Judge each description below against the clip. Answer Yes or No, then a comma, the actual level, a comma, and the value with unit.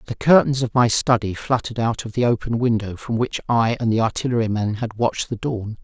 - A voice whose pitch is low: Yes, low, 115 Hz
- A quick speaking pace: Yes, fast, 215 wpm